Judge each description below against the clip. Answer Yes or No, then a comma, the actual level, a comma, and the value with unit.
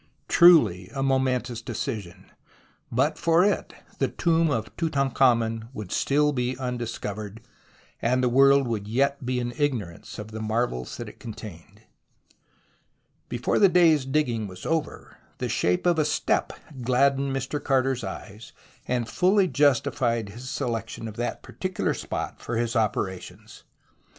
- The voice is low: Yes, low, 125 Hz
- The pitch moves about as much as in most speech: Yes, average, 3.9 semitones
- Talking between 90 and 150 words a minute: Yes, average, 140 wpm